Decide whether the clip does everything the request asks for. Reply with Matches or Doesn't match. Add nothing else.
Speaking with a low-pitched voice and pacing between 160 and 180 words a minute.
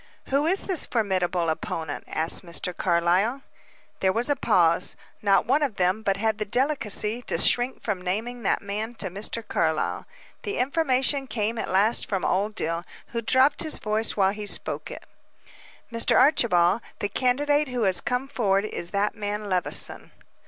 Doesn't match